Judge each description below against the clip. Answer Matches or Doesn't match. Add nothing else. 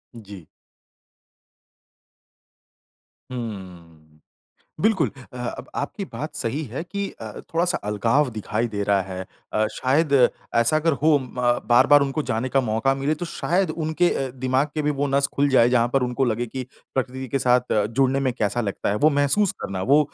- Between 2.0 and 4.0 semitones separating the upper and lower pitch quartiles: Doesn't match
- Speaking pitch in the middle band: Doesn't match